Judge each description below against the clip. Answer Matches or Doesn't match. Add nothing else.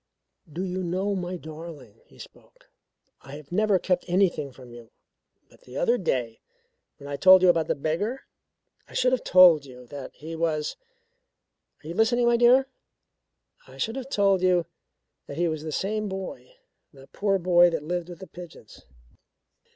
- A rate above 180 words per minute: Doesn't match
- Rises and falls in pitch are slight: Doesn't match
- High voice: Doesn't match